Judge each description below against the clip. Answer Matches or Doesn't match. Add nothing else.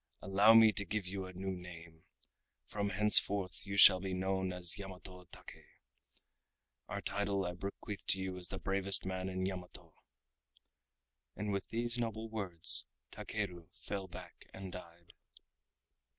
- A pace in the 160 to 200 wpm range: Doesn't match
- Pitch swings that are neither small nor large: Doesn't match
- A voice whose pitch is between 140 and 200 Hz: Doesn't match